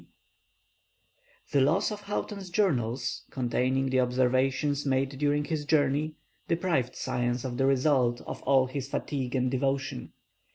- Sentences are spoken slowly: Yes, slow, 130 wpm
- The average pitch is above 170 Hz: No, low, 135 Hz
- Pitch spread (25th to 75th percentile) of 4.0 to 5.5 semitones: No, narrow, 2.5 semitones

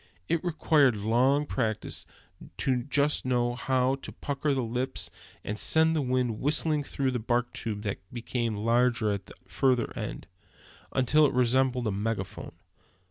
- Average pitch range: Yes, average, 3.1 semitones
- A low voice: Yes, low, 125 Hz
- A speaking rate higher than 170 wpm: No, average, 155 wpm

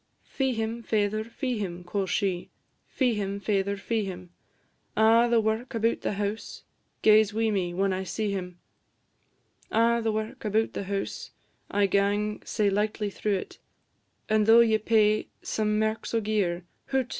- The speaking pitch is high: Yes, high, 210 Hz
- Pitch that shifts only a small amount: Yes, narrow, 2.0 semitones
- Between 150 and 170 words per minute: Yes, average, 160 wpm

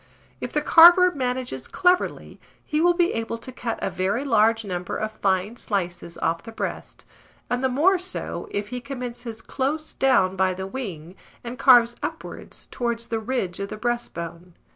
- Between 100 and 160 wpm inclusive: No, average, 170 wpm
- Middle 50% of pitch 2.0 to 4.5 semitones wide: No, wide, 5.4 semitones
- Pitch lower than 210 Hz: No, high, 235 Hz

